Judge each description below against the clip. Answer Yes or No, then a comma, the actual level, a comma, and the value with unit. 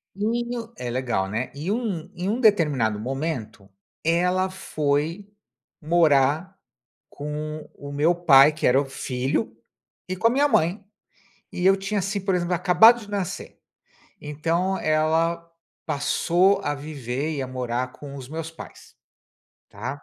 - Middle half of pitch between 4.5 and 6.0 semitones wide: Yes, average, 5.2 semitones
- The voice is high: No, medium, 160 Hz